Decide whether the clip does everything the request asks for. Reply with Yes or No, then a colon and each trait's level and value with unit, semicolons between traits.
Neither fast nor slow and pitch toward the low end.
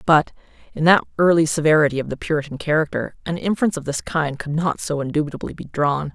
No: average, 195 wpm; medium, 155 Hz